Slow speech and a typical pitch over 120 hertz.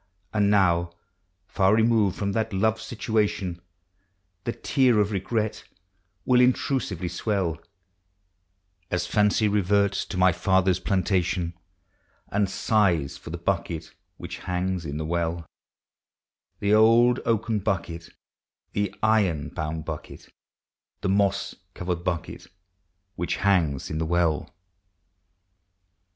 No: slow, 110 wpm; very low, 95 Hz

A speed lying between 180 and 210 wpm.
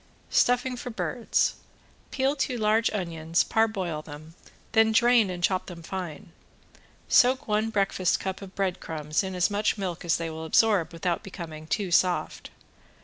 No: average, 155 wpm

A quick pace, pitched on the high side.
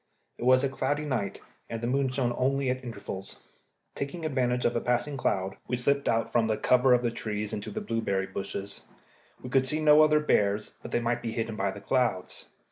No: fast, 210 wpm; low, 120 Hz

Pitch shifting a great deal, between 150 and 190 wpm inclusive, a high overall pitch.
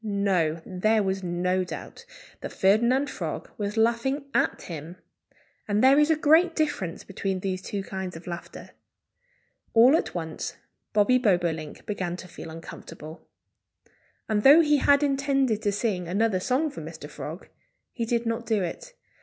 Yes: wide, 6.2 semitones; average, 155 wpm; high, 210 Hz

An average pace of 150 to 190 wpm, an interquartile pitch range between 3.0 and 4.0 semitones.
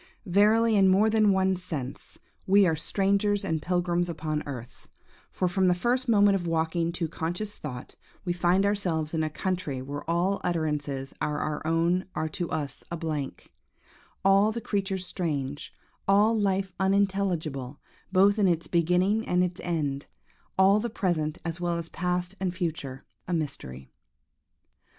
Yes: average, 160 wpm; average, 3.7 semitones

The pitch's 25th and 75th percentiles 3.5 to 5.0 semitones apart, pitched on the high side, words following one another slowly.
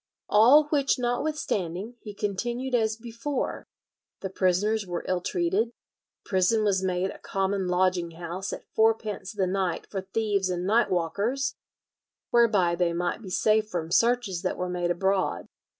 No: average, 3.8 semitones; high, 195 Hz; average, 150 wpm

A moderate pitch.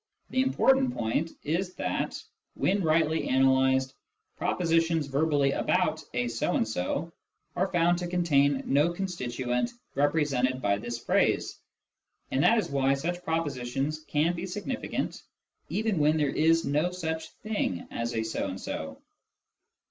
Yes: medium, 155 Hz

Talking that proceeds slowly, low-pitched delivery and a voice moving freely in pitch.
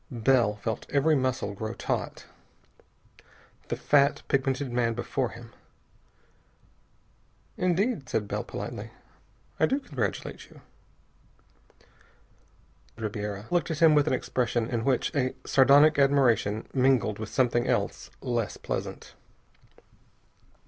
No: slow, 110 wpm; low, 130 Hz; average, 3.8 semitones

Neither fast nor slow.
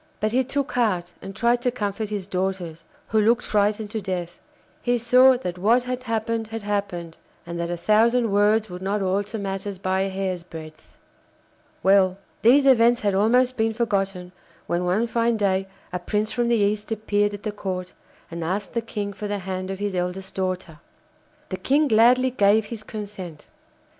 Yes: average, 185 wpm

